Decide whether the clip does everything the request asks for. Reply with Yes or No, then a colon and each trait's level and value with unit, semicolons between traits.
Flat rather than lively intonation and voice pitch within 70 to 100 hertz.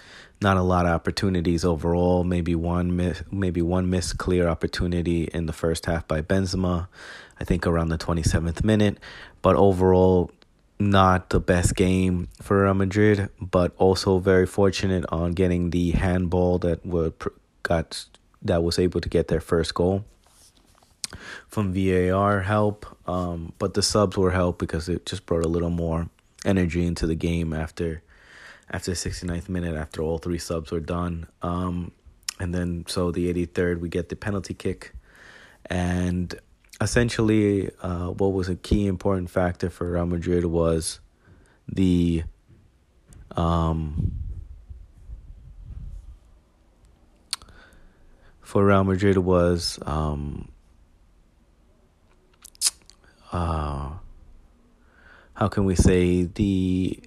Yes: narrow, 2.1 semitones; very low, 90 Hz